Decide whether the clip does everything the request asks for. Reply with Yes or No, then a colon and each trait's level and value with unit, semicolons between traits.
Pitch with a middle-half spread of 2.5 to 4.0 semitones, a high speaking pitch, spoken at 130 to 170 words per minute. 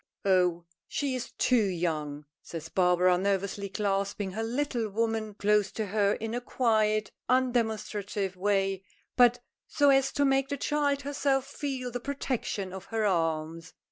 No: average, 4.8 semitones; high, 215 Hz; average, 145 wpm